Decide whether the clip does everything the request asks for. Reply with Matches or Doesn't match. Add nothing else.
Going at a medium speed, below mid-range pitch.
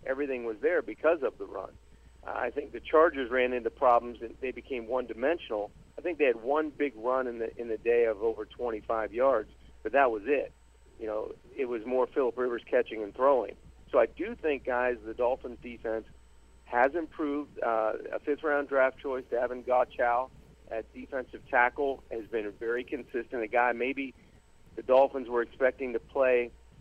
Matches